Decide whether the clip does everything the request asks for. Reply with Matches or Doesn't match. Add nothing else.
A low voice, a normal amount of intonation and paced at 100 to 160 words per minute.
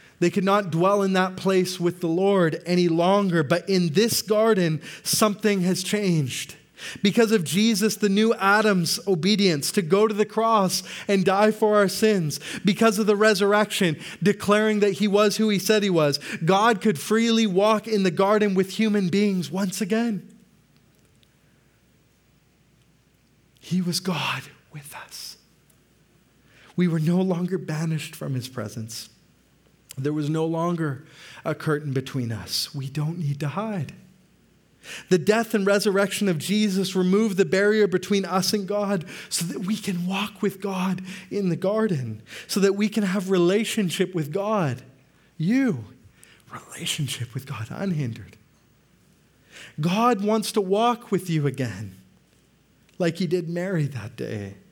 Doesn't match